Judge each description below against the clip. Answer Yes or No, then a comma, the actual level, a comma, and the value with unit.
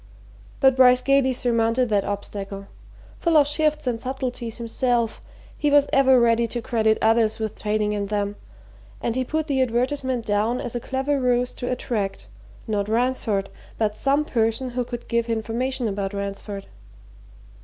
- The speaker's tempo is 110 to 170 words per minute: Yes, average, 155 wpm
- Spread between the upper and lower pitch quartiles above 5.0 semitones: No, average, 3.1 semitones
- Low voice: No, high, 235 Hz